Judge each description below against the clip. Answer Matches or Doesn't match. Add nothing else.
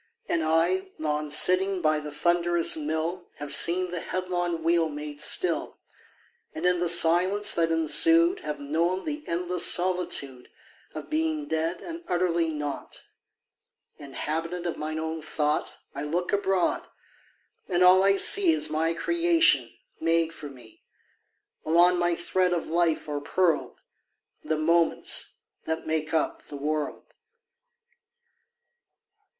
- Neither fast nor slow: Doesn't match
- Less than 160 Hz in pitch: Doesn't match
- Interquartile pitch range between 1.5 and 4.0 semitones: Matches